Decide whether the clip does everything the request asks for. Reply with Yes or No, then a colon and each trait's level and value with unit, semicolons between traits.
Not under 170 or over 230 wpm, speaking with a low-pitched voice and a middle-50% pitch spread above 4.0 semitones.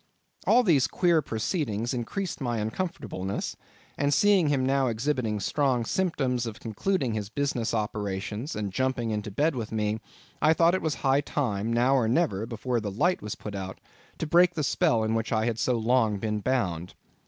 Yes: average, 180 wpm; low, 120 Hz; average, 5.2 semitones